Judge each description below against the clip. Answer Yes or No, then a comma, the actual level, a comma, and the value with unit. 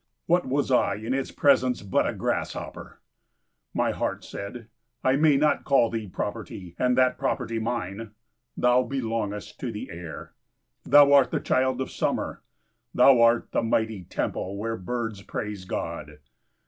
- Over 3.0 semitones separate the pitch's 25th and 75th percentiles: Yes, average, 3.9 semitones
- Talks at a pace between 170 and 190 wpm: No, average, 150 wpm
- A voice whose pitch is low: Yes, low, 115 Hz